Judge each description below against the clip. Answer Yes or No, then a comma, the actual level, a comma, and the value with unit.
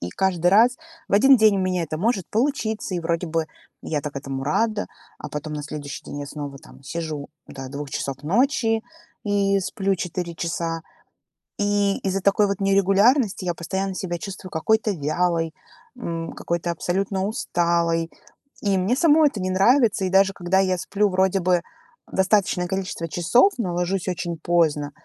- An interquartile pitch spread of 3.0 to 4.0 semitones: Yes, average, 3.3 semitones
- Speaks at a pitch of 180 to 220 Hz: Yes, medium, 185 Hz